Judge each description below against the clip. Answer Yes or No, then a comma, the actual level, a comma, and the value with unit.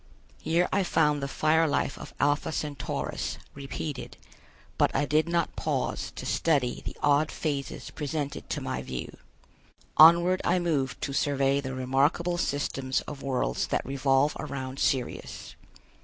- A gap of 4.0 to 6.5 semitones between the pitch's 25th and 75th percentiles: No, average, 2.8 semitones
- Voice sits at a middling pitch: Yes, medium, 145 Hz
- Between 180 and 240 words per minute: No, average, 140 wpm